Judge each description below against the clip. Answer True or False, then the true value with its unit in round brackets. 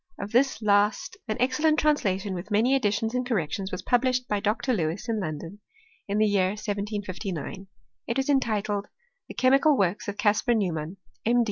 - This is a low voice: False (210 Hz)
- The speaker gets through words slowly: False (170 wpm)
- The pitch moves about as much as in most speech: True (4.2 semitones)